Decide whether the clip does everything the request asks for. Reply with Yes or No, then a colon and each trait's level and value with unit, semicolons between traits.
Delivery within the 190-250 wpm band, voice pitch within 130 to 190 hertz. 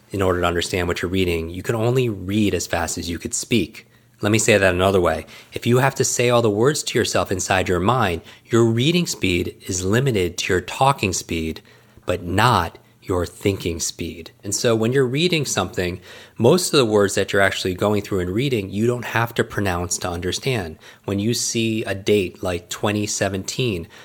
No: average, 200 wpm; low, 100 Hz